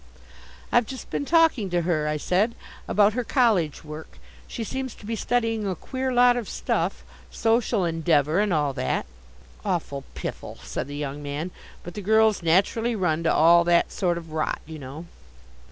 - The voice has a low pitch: No, medium, 180 Hz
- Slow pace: No, average, 175 wpm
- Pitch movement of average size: No, wide, 6.3 semitones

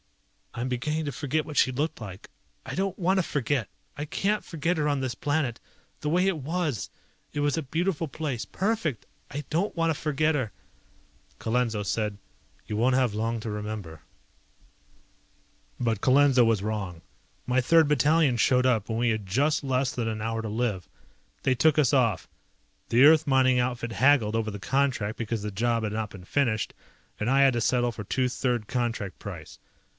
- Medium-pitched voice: No, low, 125 Hz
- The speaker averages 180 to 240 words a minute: Yes, average, 185 wpm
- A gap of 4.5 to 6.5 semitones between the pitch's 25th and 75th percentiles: Yes, average, 4.9 semitones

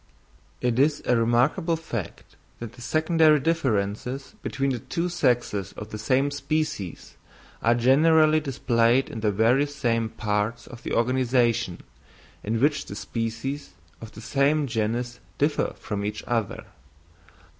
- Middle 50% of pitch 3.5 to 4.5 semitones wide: Yes, average, 4.1 semitones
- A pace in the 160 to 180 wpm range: No, slow, 135 wpm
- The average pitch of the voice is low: Yes, low, 120 Hz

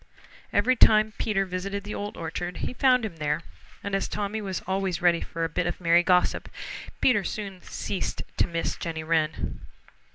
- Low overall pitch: No, high, 190 Hz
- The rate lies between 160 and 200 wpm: Yes, average, 175 wpm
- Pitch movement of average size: Yes, average, 3.5 semitones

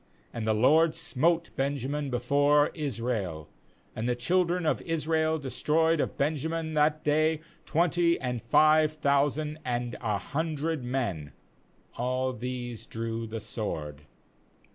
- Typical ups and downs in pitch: Yes, average, 4.6 semitones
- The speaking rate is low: Yes, slow, 125 wpm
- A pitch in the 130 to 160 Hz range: Yes, medium, 140 Hz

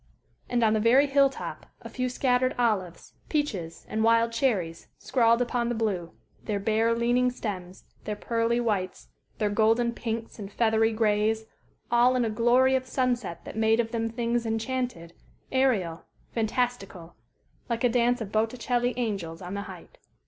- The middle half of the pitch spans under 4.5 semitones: Yes, average, 2.7 semitones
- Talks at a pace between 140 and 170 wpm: Yes, average, 160 wpm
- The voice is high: Yes, high, 230 Hz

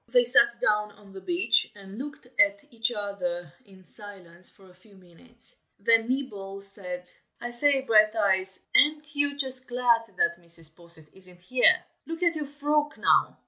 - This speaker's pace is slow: No, average, 165 wpm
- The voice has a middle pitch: No, high, 210 Hz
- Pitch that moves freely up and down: Yes, wide, 6.2 semitones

